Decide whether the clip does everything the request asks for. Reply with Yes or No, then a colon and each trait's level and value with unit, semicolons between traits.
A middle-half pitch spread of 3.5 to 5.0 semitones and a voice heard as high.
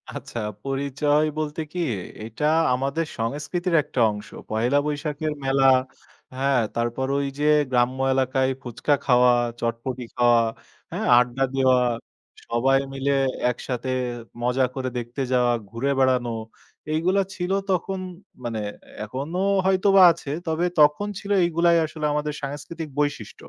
No: average, 3.8 semitones; low, 135 Hz